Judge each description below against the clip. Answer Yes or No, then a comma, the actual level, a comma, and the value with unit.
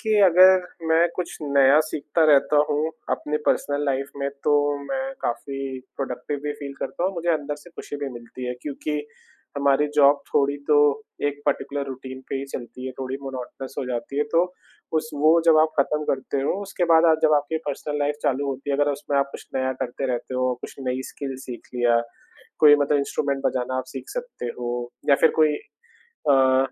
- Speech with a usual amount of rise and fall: No, narrow, 2.3 semitones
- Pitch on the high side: No, medium, 140 Hz